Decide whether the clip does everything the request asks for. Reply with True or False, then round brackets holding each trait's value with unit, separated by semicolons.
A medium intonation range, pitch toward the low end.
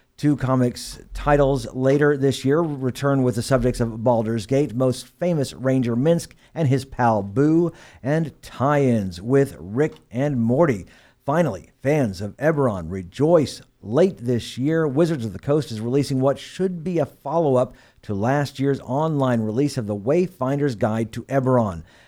True (3.7 semitones; 130 Hz)